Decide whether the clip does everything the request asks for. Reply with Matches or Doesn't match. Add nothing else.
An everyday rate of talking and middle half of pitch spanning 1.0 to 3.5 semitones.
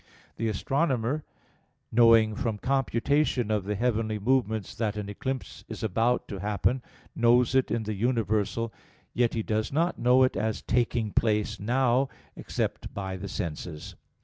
Matches